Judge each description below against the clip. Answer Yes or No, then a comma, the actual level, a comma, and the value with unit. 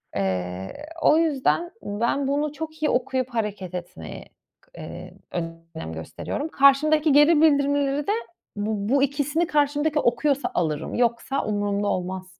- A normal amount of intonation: No, wide, 6.7 semitones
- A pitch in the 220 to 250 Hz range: No, very high, 270 Hz